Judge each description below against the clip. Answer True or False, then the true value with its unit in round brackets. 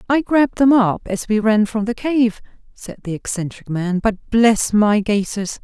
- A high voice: True (220 Hz)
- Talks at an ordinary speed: True (190 wpm)